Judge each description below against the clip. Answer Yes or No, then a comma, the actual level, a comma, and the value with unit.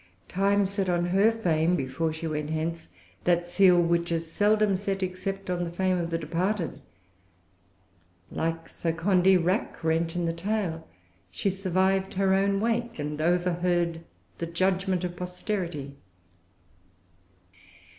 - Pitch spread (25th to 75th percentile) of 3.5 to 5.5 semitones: No, narrow, 2.6 semitones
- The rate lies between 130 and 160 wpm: Yes, slow, 135 wpm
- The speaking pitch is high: No, medium, 175 Hz